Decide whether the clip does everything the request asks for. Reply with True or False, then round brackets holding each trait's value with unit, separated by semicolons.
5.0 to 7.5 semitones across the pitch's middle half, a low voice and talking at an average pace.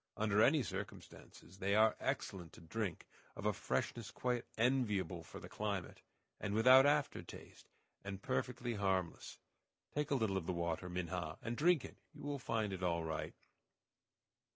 True (5.6 semitones; 105 Hz; 160 wpm)